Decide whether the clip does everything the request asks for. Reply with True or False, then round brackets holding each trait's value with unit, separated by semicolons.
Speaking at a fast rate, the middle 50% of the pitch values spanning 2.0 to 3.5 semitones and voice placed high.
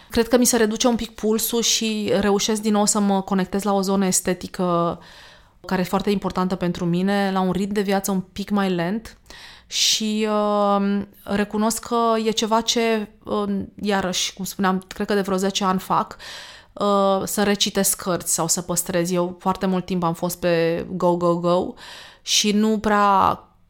True (180 wpm; 2.4 semitones; 200 Hz)